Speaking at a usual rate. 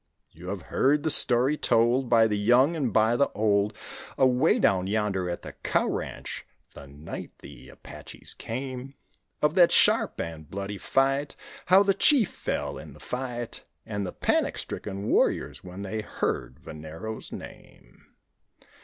Yes: average, 155 wpm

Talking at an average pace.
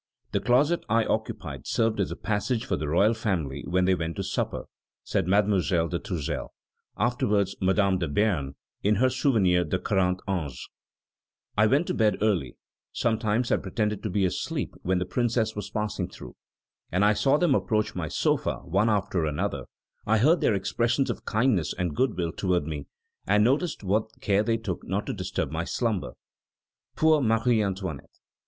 Yes: average, 175 wpm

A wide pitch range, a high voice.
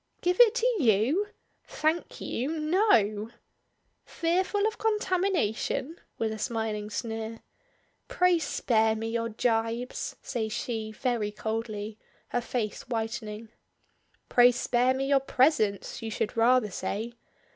Yes: wide, 5.9 semitones; high, 235 Hz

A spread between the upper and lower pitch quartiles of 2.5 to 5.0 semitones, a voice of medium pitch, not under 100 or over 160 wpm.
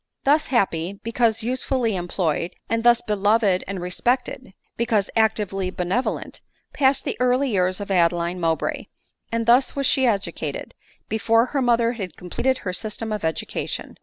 No: average, 4.7 semitones; high, 220 Hz; average, 150 wpm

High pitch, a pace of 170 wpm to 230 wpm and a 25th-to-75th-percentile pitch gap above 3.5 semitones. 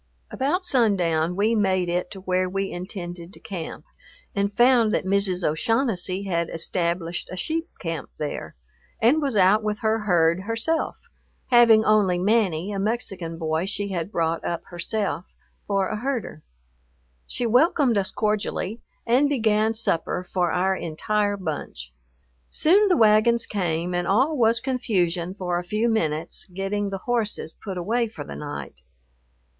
No: high, 195 Hz; average, 150 wpm; average, 4.3 semitones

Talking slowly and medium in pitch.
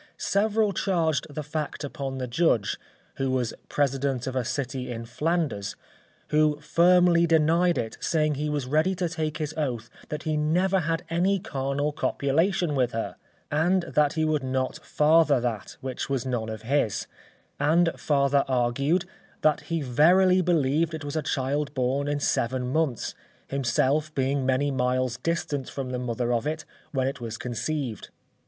No: average, 160 wpm; medium, 145 Hz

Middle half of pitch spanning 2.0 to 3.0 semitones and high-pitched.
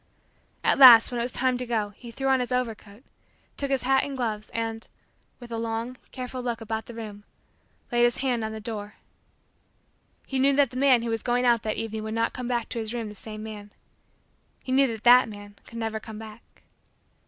Yes: narrow, 2.4 semitones; high, 230 Hz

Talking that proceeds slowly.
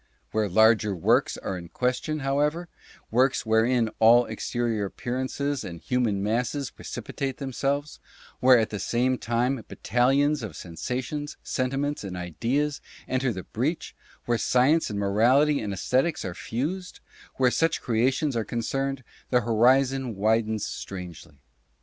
No: average, 145 wpm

